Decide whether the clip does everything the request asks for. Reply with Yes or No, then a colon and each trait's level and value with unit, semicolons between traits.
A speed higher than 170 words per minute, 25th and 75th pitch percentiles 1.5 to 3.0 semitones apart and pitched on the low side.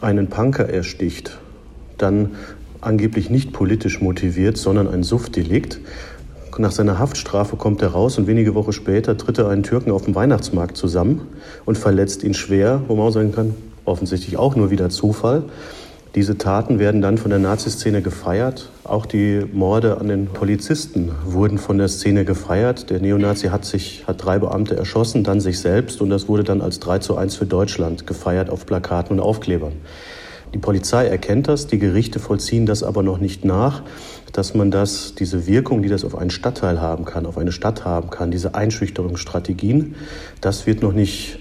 Yes: average, 180 wpm; narrow, 2.5 semitones; low, 100 Hz